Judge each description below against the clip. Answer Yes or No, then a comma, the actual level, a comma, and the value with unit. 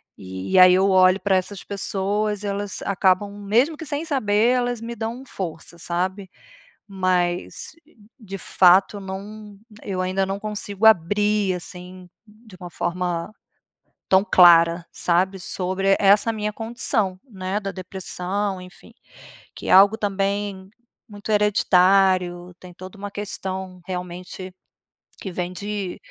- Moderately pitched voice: No, high, 195 Hz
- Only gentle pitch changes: Yes, narrow, 2.1 semitones